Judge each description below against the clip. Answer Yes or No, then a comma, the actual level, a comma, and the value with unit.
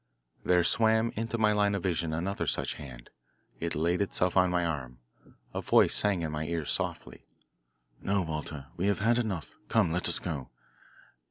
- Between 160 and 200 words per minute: Yes, average, 175 wpm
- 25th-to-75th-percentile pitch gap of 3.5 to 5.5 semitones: Yes, average, 4.3 semitones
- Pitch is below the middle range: Yes, very low, 90 Hz